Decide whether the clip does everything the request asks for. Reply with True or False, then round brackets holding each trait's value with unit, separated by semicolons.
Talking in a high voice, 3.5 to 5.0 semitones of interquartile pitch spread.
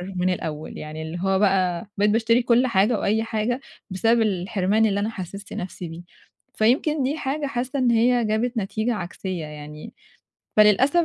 True (215 Hz; 4.4 semitones)